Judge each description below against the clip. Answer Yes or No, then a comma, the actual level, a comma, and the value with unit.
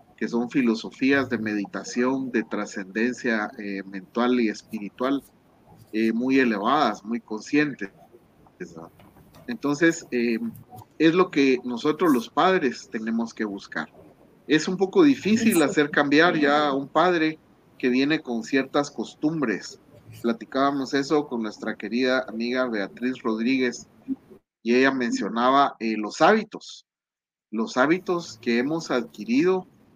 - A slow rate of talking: Yes, slow, 120 wpm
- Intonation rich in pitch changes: No, average, 4.8 semitones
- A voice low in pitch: Yes, low, 125 Hz